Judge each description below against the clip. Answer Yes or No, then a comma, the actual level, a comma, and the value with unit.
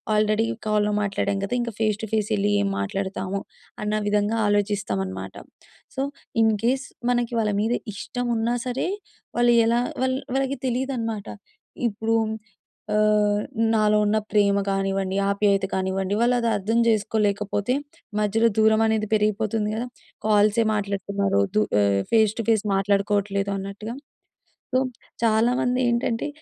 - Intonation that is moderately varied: No, narrow, 2.3 semitones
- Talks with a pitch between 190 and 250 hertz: Yes, high, 210 Hz